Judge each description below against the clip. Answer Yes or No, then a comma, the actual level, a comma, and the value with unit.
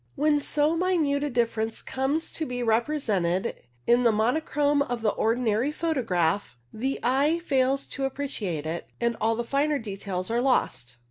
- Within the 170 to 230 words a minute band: No, average, 155 wpm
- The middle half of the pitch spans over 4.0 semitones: Yes, average, 4.6 semitones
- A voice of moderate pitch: No, high, 245 Hz